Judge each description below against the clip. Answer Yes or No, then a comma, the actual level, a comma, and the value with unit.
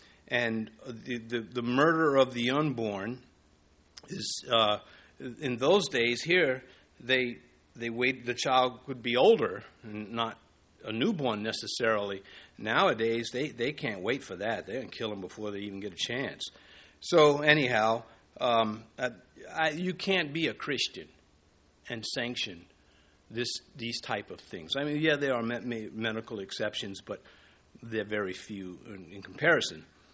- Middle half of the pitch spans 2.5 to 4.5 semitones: Yes, average, 3.8 semitones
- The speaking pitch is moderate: No, low, 115 Hz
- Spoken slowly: No, average, 150 wpm